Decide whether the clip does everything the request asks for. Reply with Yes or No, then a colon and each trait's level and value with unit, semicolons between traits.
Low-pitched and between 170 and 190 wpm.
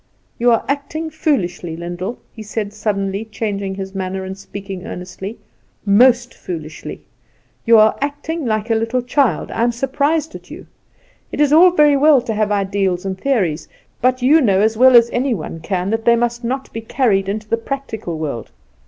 No: high, 225 Hz; average, 180 wpm